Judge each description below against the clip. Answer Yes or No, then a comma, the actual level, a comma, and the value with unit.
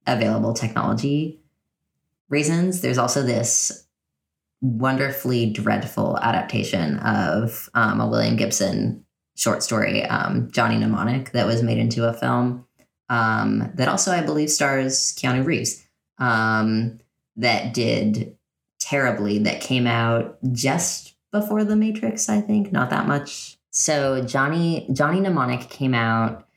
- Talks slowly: Yes, slow, 125 wpm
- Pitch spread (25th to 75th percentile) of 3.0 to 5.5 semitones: Yes, average, 4.2 semitones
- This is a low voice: Yes, low, 125 Hz